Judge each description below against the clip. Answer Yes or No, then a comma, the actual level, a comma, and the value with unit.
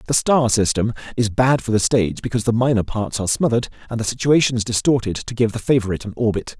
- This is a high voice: No, low, 115 Hz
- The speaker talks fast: Yes, fast, 220 wpm